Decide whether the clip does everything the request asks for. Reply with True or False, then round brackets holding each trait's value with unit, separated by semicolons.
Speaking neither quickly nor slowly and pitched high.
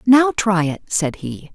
True (195 wpm; 200 Hz)